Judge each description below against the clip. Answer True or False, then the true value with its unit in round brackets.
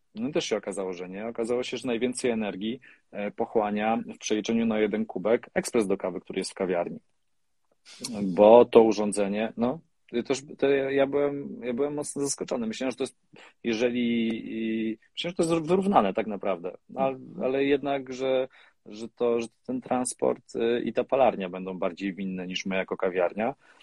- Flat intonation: False (3.8 semitones)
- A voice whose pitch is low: True (120 Hz)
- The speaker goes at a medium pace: False (170 wpm)